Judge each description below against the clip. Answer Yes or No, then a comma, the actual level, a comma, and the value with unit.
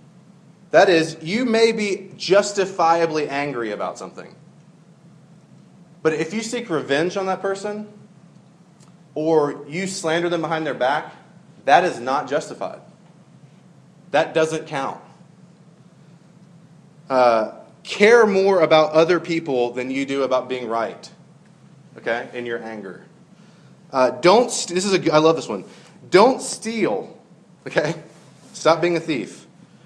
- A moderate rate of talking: No, slow, 130 wpm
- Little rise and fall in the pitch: Yes, narrow, 2.3 semitones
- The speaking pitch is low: No, medium, 170 Hz